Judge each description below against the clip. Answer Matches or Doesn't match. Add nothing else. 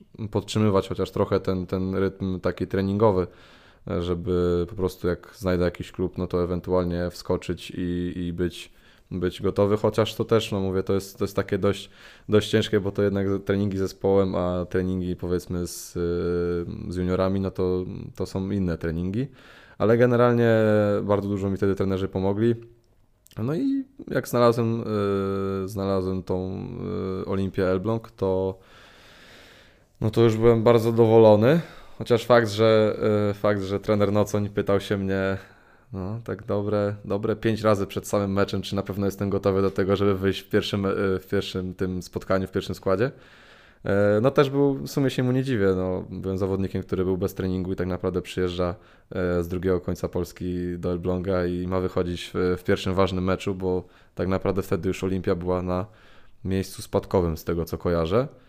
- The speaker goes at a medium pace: Doesn't match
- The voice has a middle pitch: Doesn't match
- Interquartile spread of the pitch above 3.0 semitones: Doesn't match